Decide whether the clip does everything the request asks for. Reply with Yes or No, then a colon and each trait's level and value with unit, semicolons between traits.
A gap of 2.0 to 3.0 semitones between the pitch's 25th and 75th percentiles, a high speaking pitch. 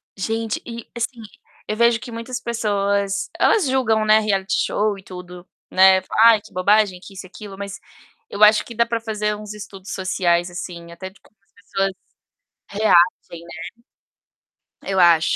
Yes: average, 2.7 semitones; high, 205 Hz